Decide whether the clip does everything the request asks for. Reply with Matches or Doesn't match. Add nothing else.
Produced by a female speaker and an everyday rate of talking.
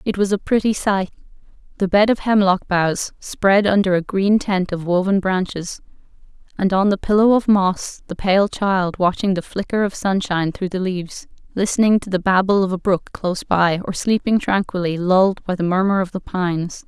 Matches